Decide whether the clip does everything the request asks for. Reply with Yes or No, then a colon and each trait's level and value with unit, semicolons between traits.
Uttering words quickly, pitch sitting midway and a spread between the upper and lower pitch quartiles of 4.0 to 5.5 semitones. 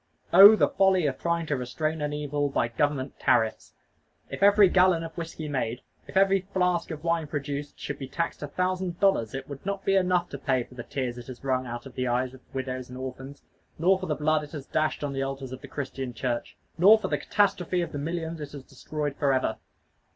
Yes: fast, 225 wpm; medium, 145 Hz; average, 4.8 semitones